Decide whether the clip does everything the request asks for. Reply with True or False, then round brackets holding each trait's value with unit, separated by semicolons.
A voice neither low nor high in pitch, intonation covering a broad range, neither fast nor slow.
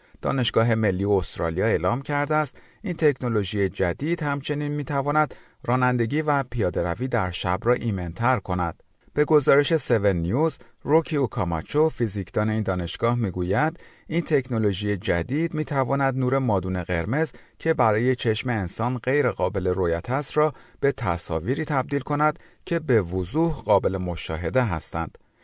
False (125 Hz; 6.6 semitones; 130 wpm)